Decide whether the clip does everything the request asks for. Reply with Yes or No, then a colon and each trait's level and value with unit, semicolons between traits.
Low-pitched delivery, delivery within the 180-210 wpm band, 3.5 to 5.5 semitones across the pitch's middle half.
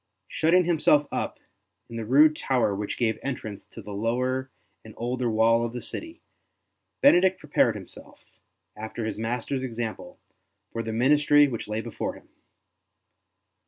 No: low, 120 Hz; average, 145 wpm; average, 4.5 semitones